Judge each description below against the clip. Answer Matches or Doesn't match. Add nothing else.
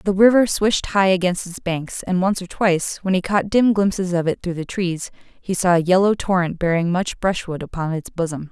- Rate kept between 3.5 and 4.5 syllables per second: Doesn't match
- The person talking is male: Doesn't match